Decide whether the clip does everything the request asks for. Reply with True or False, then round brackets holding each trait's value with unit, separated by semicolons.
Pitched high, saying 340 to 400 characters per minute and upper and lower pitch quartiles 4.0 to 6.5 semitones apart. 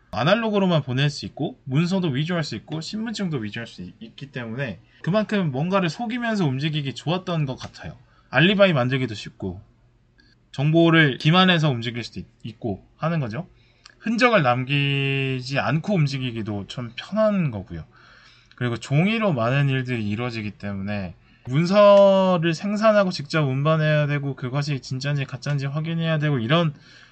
False (140 Hz; 345 characters per minute; 5.6 semitones)